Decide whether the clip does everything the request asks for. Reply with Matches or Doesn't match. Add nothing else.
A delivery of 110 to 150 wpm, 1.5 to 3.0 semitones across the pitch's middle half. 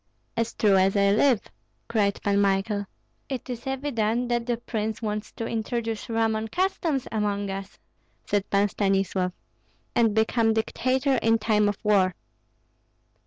Matches